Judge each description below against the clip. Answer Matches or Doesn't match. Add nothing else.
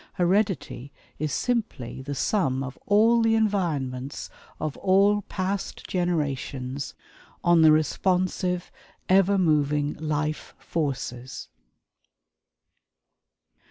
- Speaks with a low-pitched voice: Doesn't match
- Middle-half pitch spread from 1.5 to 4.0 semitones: Doesn't match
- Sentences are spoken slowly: Matches